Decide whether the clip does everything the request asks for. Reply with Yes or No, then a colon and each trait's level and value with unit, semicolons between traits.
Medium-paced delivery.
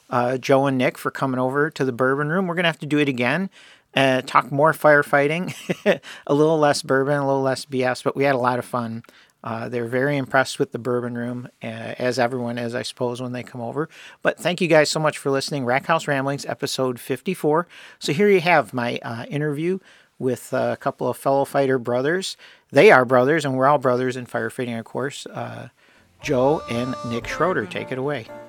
No: fast, 215 wpm